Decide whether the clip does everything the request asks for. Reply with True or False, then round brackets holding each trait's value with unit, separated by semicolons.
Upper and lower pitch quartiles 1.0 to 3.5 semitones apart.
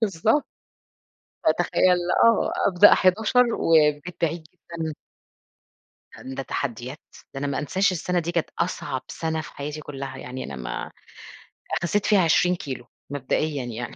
False (4.7 semitones)